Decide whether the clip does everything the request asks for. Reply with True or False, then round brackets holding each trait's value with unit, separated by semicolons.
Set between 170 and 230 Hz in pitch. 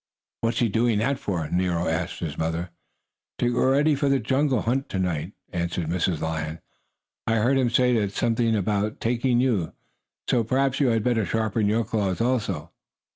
False (110 Hz)